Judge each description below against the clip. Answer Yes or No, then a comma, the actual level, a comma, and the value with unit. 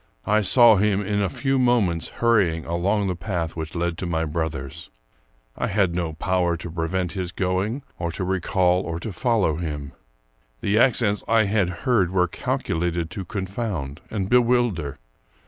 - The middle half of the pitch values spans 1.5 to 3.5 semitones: No, average, 3.9 semitones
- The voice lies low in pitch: Yes, very low, 95 Hz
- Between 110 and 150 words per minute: No, average, 165 wpm